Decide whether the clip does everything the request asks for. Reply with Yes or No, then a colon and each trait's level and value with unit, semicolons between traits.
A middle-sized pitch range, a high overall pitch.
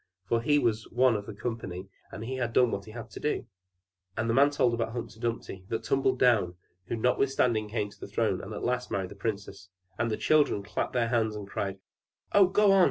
No: average, 3.0 semitones; low, 115 Hz